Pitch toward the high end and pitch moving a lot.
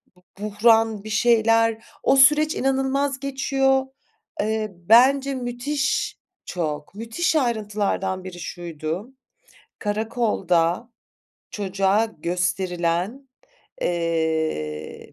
Yes: high, 215 Hz; wide, 6.6 semitones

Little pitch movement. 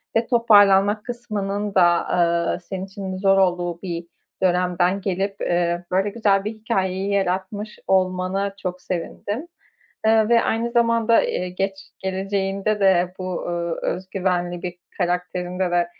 Yes: narrow, 2.2 semitones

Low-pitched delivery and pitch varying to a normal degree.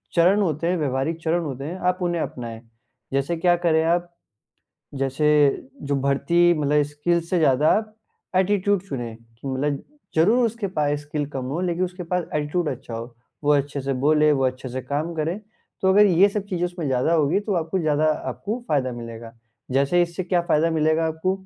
No: medium, 155 Hz; average, 4.2 semitones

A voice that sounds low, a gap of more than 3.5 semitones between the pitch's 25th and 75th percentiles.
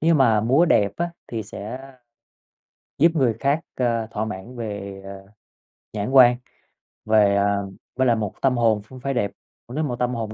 Yes: low, 115 Hz; average, 3.9 semitones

